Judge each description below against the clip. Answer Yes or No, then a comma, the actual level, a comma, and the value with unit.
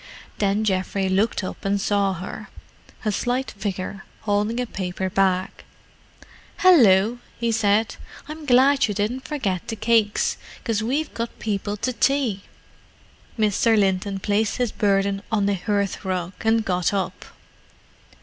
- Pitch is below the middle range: No, high, 205 Hz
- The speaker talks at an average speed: No, slow, 130 wpm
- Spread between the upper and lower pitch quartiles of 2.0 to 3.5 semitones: Yes, average, 2.9 semitones